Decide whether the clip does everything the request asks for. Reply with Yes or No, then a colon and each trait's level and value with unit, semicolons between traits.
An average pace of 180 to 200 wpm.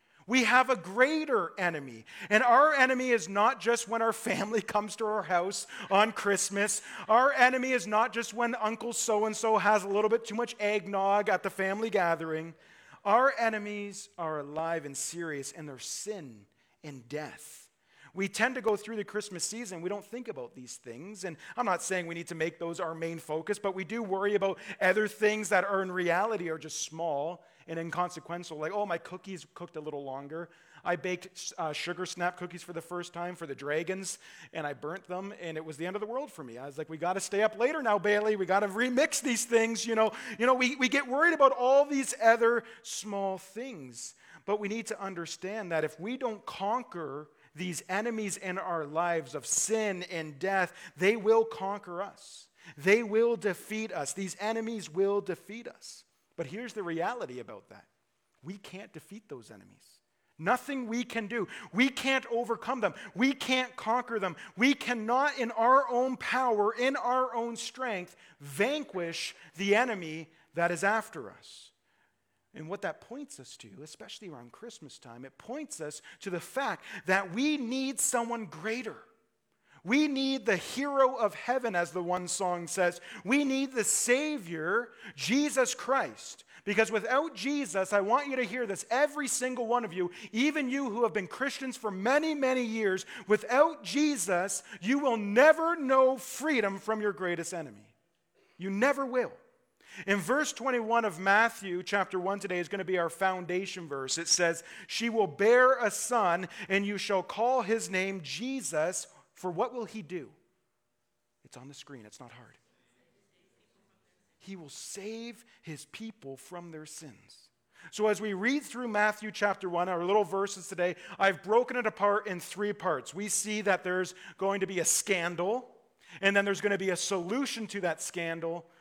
Yes: average, 185 wpm